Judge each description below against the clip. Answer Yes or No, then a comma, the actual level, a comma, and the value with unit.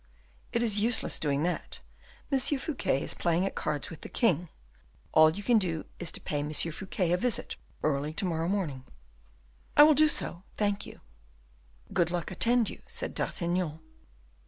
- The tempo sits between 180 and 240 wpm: No, average, 170 wpm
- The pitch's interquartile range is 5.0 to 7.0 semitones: Yes, wide, 5.6 semitones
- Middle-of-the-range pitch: Yes, medium, 180 Hz